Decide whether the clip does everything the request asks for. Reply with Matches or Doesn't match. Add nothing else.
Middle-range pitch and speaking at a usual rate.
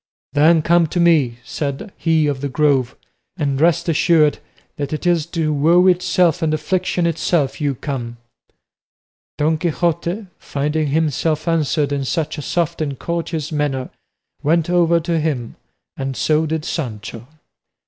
Matches